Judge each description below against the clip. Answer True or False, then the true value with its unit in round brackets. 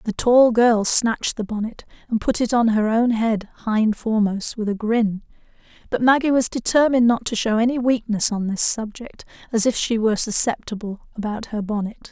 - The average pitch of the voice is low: False (225 Hz)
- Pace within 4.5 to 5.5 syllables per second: True (5.2 syllables/s)